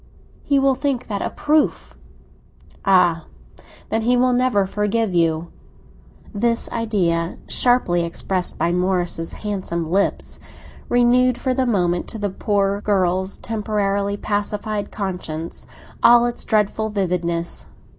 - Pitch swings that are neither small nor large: Yes, average, 4.5 semitones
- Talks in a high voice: Yes, high, 205 Hz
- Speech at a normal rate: No, slow, 120 wpm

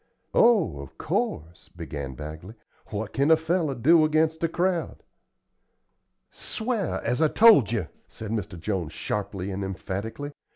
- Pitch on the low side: Yes, low, 115 Hz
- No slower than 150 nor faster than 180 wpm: No, slow, 135 wpm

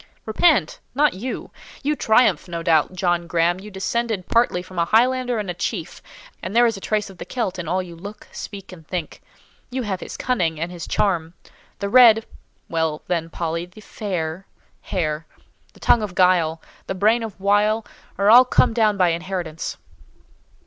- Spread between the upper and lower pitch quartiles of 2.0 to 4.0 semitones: No, average, 4.5 semitones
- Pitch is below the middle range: No, high, 190 Hz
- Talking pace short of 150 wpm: No, average, 175 wpm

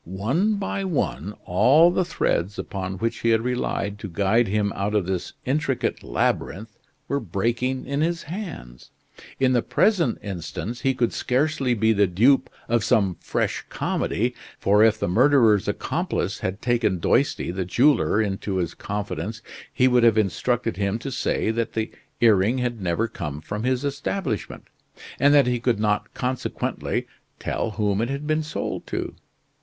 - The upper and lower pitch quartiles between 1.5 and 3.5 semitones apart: No, average, 4.6 semitones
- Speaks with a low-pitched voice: Yes, low, 115 Hz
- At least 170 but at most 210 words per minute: No, average, 160 wpm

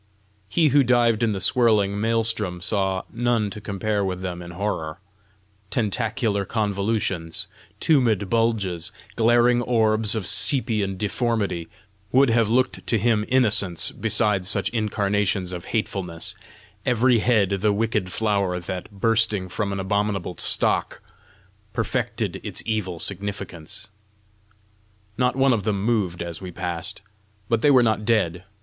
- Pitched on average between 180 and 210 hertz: No, low, 105 Hz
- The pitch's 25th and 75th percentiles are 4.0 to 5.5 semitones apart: No, average, 3.2 semitones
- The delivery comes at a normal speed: No, slow, 130 wpm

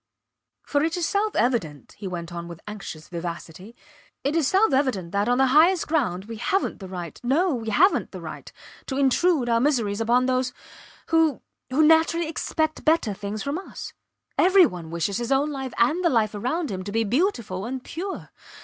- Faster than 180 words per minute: Yes, average, 190 wpm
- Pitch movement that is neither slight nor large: No, wide, 7.7 semitones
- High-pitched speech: Yes, very high, 250 Hz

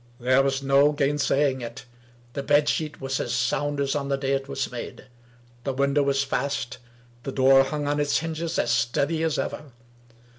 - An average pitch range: No, narrow, 1.4 semitones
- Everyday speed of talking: Yes, average, 185 wpm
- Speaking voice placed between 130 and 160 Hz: Yes, medium, 140 Hz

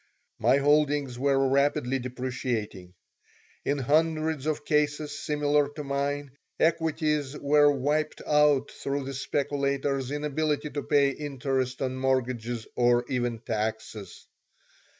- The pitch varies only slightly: Yes, narrow, 2.3 semitones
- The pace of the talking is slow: Yes, slow, 110 wpm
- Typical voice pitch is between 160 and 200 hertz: No, medium, 140 Hz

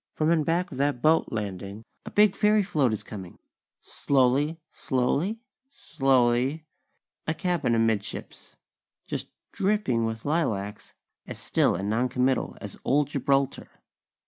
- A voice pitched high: No, low, 135 Hz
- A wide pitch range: Yes, wide, 5.8 semitones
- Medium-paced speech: No, slow, 130 wpm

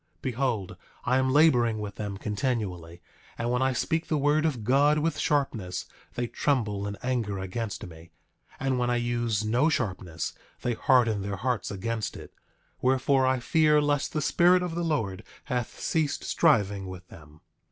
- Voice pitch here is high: No, low, 120 Hz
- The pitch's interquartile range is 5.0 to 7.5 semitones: Yes, wide, 5.6 semitones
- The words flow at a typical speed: Yes, average, 170 wpm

